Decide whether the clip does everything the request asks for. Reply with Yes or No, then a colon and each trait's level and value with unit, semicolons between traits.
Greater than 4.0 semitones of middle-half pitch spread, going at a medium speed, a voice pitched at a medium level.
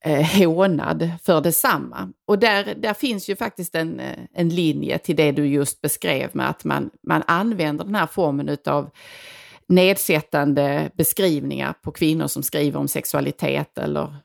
Yes: average, 5.3 semitones; average, 145 wpm; medium, 165 Hz